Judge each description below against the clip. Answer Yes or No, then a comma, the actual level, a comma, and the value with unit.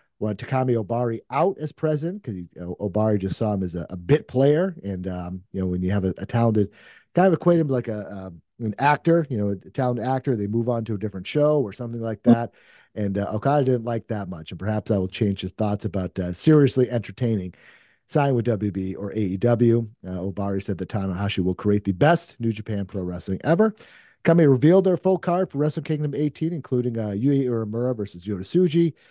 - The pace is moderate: No, fast, 215 wpm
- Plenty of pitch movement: Yes, wide, 6.0 semitones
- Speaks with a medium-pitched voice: No, low, 115 Hz